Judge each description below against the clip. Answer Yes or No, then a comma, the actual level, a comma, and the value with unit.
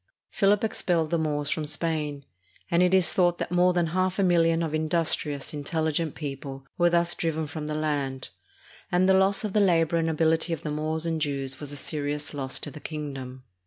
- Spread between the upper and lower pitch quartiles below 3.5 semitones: Yes, average, 2.8 semitones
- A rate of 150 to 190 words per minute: No, fast, 205 wpm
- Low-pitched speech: No, medium, 160 Hz